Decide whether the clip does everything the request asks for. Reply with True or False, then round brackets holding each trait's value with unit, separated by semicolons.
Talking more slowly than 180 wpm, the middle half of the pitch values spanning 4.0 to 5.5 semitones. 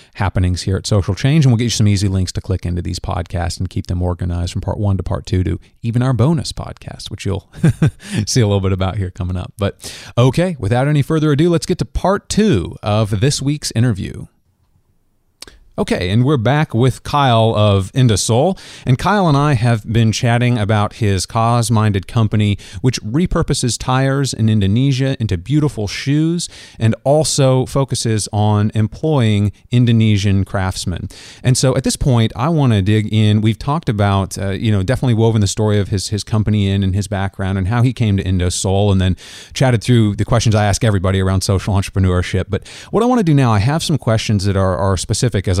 False (200 wpm; 4.7 semitones)